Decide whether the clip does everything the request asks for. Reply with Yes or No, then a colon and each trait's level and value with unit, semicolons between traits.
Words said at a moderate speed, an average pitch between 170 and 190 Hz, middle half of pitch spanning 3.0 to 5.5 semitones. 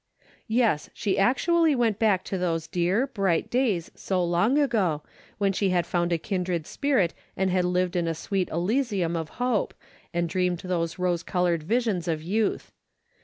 Yes: average, 170 wpm; medium, 185 Hz; average, 4.2 semitones